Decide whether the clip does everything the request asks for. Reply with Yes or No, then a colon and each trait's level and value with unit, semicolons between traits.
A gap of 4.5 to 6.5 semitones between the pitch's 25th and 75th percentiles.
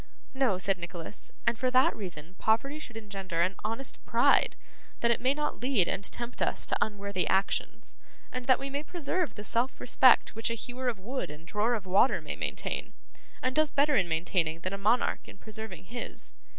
Yes: average, 5.3 semitones